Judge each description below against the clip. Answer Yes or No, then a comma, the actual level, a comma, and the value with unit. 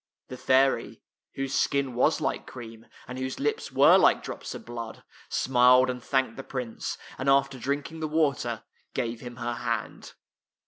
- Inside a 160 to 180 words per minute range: Yes, average, 165 wpm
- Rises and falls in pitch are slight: Yes, narrow, 2.3 semitones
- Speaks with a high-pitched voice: No, low, 130 Hz